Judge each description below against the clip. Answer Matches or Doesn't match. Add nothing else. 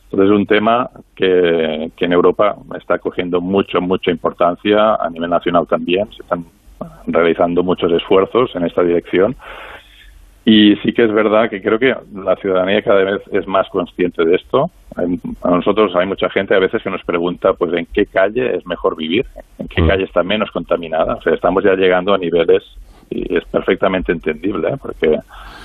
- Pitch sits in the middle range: Doesn't match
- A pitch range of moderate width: Matches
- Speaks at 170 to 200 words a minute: Matches